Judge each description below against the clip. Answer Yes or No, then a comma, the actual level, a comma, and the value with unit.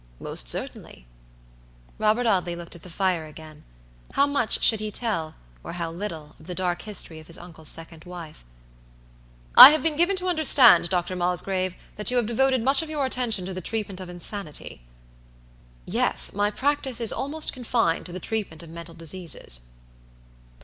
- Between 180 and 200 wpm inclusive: No, average, 170 wpm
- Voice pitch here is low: No, medium, 185 Hz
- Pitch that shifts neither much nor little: No, wide, 6.3 semitones